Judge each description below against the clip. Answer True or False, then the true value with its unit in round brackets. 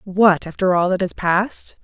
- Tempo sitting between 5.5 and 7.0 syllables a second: False (4.7 syllables/s)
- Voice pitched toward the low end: False (190 Hz)